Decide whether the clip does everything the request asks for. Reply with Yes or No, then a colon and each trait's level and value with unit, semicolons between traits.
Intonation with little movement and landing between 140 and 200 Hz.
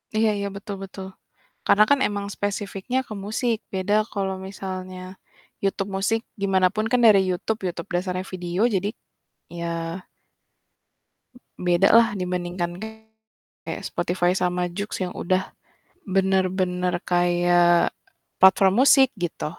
Yes: narrow, 2.1 semitones; high, 190 Hz